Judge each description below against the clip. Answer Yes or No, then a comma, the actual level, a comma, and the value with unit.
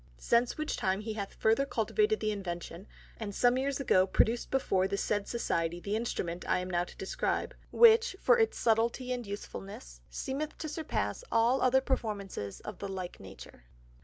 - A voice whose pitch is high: Yes, high, 220 Hz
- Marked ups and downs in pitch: Yes, wide, 5.7 semitones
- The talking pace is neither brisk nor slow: Yes, average, 175 wpm